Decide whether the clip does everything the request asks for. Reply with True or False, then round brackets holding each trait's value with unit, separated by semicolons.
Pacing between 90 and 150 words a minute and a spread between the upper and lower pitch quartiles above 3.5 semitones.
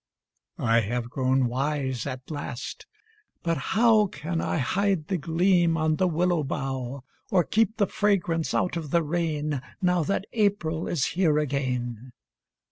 True (145 wpm; 5.1 semitones)